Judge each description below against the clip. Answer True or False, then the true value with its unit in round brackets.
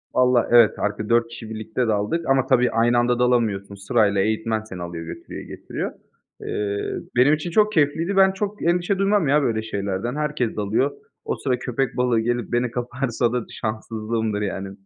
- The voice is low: True (120 Hz)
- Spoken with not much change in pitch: False (3.9 semitones)